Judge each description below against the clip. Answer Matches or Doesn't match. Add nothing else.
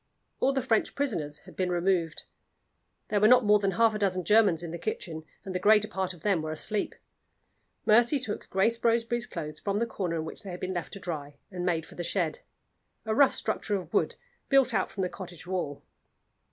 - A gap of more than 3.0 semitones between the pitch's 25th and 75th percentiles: Matches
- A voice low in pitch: Doesn't match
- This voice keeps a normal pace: Doesn't match